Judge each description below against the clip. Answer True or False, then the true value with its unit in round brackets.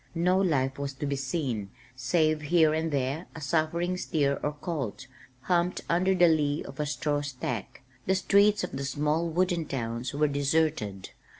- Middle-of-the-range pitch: True (150 Hz)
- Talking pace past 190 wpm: False (170 wpm)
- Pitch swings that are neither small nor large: True (3.6 semitones)